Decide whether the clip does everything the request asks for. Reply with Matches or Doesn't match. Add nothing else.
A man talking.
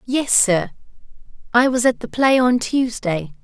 Doesn't match